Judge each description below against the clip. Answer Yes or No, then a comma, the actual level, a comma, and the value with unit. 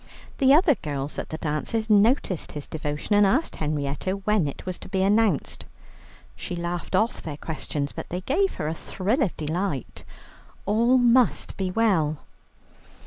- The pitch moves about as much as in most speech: No, wide, 6.6 semitones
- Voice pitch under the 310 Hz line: Yes, medium, 185 Hz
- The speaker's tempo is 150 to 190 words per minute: Yes, average, 160 wpm